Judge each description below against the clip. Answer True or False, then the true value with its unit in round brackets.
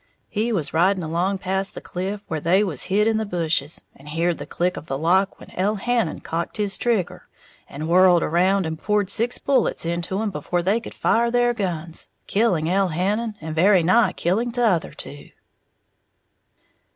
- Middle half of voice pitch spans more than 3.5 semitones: True (3.9 semitones)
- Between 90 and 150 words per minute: False (175 wpm)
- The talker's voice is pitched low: False (185 Hz)